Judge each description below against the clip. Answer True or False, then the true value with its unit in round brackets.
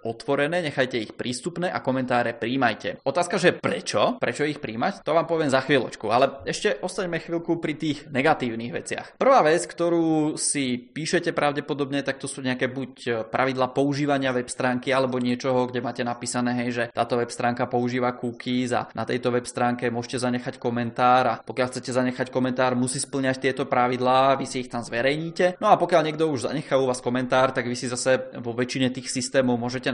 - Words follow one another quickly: True (185 wpm)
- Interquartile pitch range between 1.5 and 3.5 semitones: True (2.6 semitones)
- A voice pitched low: True (130 Hz)